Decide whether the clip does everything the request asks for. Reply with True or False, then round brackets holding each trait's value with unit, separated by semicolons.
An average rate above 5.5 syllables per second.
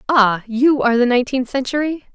True (5.9 syllables/s)